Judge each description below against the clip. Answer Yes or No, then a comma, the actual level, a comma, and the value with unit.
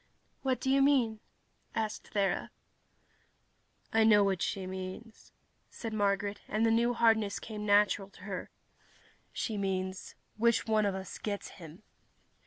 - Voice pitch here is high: Yes, high, 210 Hz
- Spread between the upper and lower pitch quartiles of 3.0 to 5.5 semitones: No, narrow, 2.4 semitones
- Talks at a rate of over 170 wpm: No, average, 140 wpm